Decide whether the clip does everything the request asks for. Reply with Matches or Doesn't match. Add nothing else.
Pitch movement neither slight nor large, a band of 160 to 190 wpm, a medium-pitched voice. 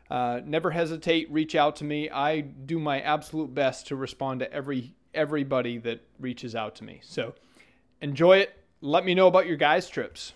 Matches